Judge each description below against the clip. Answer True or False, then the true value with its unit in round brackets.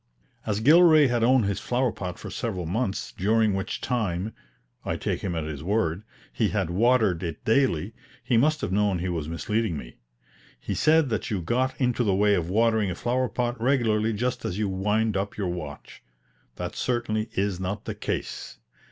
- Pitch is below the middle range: True (105 Hz)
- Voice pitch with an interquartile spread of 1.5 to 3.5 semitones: False (4.6 semitones)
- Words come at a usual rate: True (185 wpm)